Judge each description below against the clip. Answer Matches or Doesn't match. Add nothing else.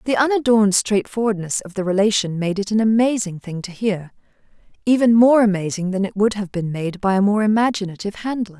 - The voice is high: Matches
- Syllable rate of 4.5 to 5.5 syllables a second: Doesn't match